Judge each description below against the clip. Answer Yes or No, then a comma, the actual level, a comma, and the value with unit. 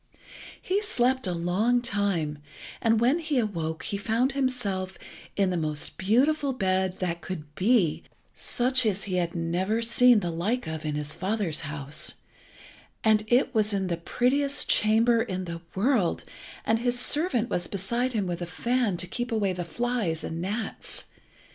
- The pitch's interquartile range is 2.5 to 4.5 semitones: No, wide, 5.6 semitones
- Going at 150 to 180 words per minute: Yes, average, 165 wpm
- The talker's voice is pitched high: Yes, high, 205 Hz